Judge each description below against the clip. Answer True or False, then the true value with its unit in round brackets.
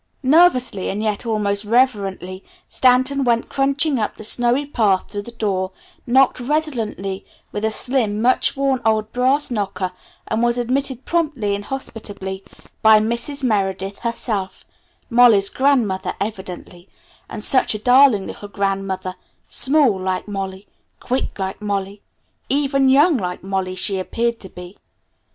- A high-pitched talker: True (220 Hz)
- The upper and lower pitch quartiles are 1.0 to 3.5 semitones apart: False (4.8 semitones)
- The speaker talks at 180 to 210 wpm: False (135 wpm)